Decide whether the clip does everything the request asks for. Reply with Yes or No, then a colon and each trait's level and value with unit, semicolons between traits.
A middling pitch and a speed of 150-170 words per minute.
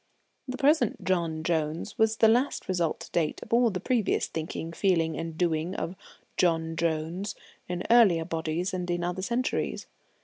Yes: medium, 175 Hz; average, 165 wpm